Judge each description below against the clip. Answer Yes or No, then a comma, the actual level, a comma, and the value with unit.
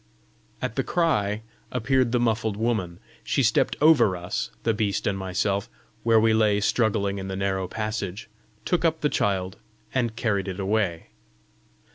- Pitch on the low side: Yes, low, 105 Hz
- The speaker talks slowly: No, average, 155 wpm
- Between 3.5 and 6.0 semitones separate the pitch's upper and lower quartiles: No, average, 3.0 semitones